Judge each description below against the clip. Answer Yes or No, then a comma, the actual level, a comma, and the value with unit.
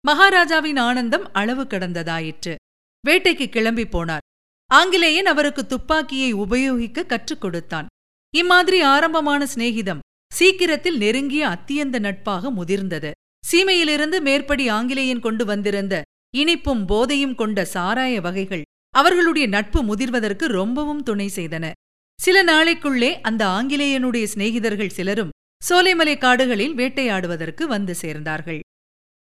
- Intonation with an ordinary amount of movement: No, wide, 6.9 semitones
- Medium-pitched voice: No, very high, 250 Hz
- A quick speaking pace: No, average, 100 wpm